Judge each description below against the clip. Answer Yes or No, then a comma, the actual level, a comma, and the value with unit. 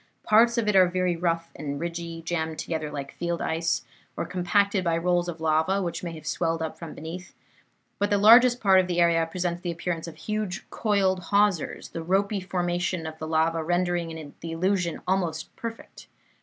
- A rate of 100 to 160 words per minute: No, average, 185 wpm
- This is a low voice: No, medium, 175 Hz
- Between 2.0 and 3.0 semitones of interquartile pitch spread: Yes, narrow, 2.5 semitones